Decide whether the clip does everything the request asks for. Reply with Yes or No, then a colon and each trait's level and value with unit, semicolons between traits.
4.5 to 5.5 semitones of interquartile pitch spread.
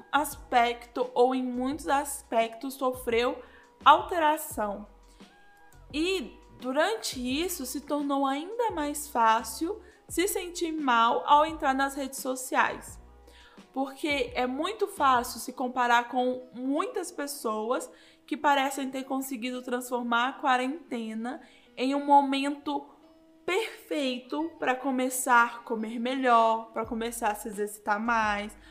No: average, 3.5 semitones